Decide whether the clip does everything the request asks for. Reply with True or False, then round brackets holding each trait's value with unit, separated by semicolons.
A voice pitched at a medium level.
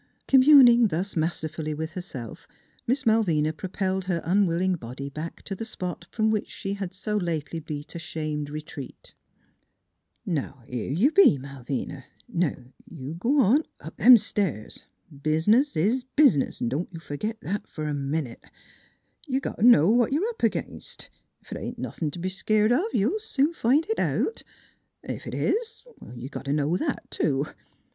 True (180 Hz)